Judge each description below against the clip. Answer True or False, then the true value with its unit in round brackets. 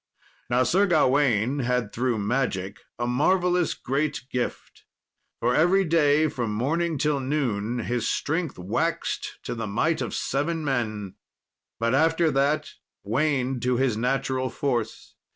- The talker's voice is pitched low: True (130 Hz)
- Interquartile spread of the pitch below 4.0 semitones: False (4.3 semitones)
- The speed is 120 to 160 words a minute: True (135 wpm)